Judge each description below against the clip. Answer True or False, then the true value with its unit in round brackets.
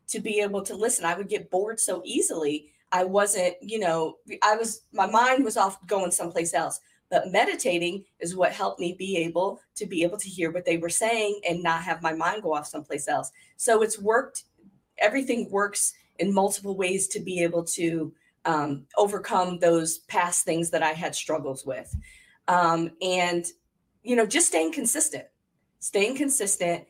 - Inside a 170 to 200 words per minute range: True (180 wpm)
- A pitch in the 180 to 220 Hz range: True (185 Hz)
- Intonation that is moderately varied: True (3.8 semitones)